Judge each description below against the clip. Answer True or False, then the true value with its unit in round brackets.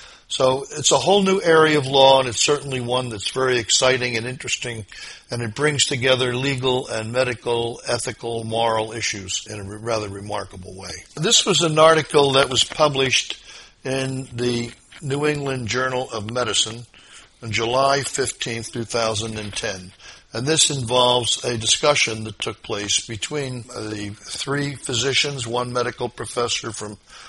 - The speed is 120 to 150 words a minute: True (145 wpm)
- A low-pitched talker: True (125 Hz)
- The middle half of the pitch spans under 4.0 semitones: True (3.2 semitones)